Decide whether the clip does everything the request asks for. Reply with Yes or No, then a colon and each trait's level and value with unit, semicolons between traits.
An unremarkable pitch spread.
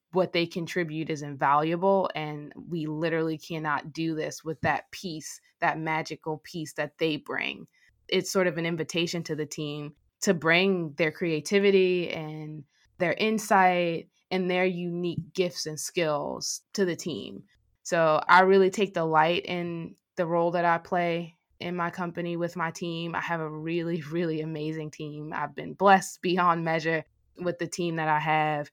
No: narrow, 2.3 semitones